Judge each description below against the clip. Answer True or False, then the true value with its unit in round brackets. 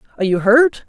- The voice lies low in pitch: False (235 Hz)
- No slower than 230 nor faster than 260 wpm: False (205 wpm)